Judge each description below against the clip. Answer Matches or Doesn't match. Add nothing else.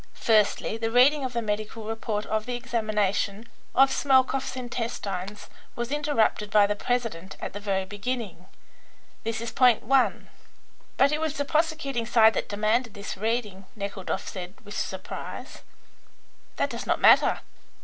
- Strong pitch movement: Doesn't match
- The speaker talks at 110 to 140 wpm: Doesn't match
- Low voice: Doesn't match